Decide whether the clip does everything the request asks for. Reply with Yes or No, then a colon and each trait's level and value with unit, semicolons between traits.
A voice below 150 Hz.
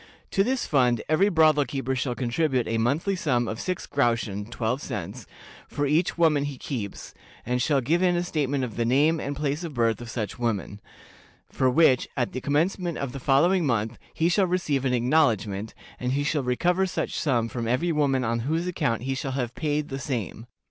Yes: low, 135 Hz